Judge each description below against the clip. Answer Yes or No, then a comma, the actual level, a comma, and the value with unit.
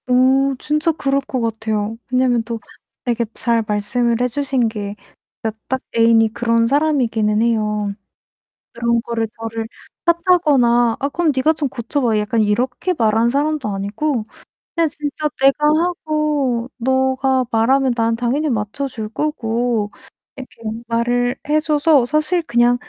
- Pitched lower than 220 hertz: No, high, 245 Hz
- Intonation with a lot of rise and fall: No, average, 4.0 semitones